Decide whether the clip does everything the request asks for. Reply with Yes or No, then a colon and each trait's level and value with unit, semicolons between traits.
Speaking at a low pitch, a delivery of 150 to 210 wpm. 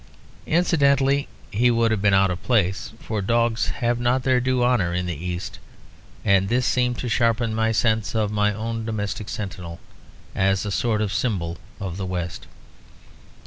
Yes: low, 110 Hz; average, 170 wpm